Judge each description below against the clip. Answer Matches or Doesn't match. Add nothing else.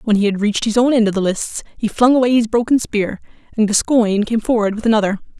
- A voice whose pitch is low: Doesn't match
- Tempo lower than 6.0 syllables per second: Doesn't match